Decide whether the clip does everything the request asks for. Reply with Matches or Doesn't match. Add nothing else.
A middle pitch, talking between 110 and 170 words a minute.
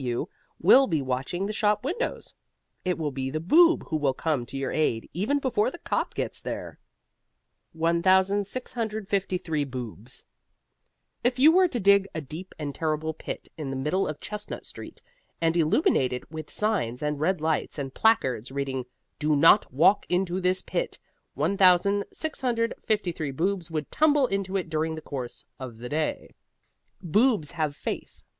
Matches